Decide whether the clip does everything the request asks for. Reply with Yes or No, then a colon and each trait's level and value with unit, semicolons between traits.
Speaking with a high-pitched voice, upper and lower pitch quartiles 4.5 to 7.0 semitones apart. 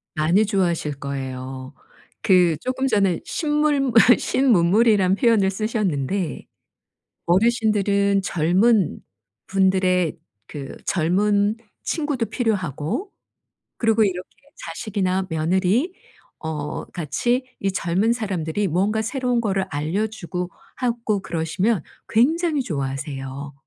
Yes: high, 195 Hz; wide, 5.4 semitones